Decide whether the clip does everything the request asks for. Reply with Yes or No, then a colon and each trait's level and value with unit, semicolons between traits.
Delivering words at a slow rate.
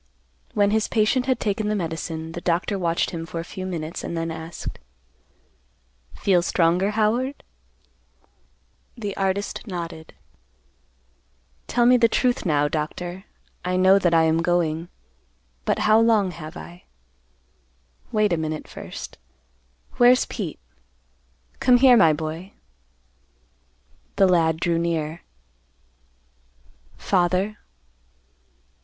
Yes: slow, 115 wpm